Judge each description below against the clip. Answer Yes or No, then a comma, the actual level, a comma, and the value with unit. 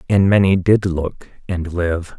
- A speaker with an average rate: Yes, average, 165 wpm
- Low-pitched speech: Yes, very low, 90 Hz